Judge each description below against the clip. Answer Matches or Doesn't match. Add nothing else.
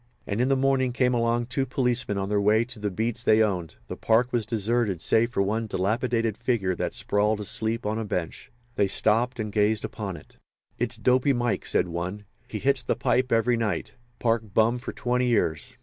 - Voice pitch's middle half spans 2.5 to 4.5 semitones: Matches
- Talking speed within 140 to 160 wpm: Doesn't match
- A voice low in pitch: Matches